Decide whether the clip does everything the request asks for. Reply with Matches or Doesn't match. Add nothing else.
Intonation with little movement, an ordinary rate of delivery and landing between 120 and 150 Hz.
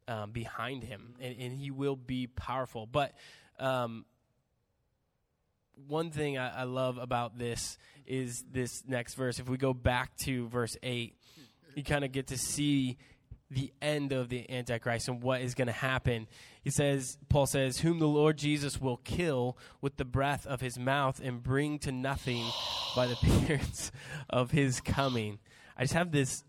Matches